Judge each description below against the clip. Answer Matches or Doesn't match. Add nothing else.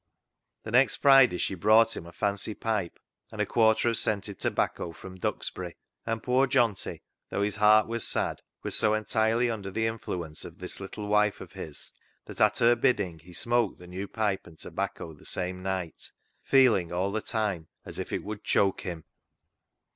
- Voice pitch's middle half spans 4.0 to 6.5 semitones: Doesn't match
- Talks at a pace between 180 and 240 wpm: Matches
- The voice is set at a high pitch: Doesn't match